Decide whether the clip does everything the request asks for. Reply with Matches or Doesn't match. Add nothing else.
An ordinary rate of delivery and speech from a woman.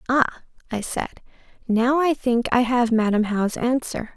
Matches